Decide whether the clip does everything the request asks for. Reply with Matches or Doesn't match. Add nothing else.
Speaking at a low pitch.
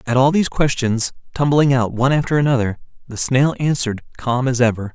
Matches